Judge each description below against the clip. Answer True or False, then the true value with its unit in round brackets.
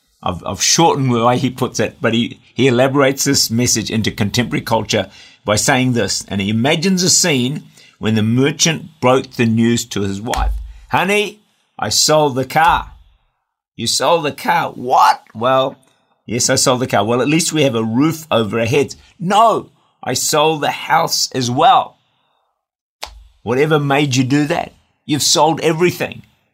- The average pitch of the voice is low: True (130 Hz)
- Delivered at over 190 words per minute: False (170 wpm)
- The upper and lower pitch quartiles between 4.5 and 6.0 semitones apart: True (4.9 semitones)